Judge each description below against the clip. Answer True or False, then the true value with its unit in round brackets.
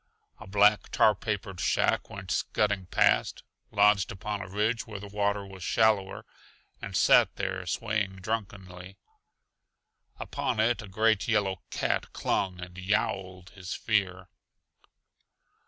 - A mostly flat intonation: True (2.0 semitones)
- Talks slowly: True (125 wpm)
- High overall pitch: False (100 Hz)